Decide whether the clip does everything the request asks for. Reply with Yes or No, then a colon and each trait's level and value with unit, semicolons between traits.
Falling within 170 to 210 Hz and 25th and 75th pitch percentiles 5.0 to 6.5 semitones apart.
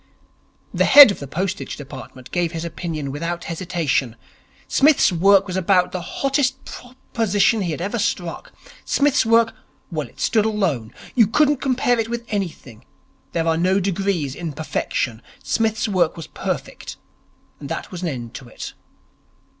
Yes: medium, 185 Hz; wide, 5.6 semitones